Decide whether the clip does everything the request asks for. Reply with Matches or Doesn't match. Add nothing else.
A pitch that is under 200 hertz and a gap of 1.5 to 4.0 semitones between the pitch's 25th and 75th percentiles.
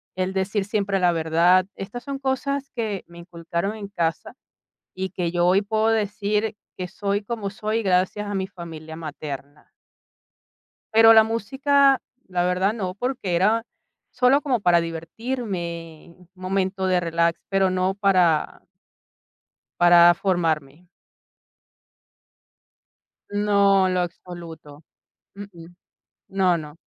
Matches